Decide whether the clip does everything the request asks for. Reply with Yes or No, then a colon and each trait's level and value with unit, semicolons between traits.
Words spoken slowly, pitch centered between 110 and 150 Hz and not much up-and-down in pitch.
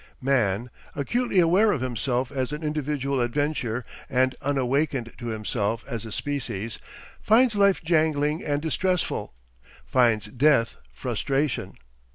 No: slow, 120 wpm; low, 135 Hz; average, 4.2 semitones